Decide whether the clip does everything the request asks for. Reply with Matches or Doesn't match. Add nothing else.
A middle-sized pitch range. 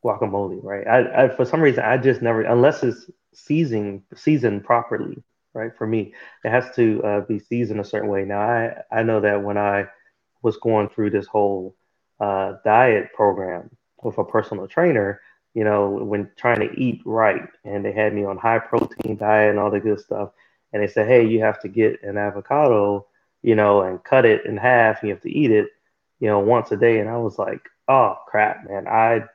Doesn't match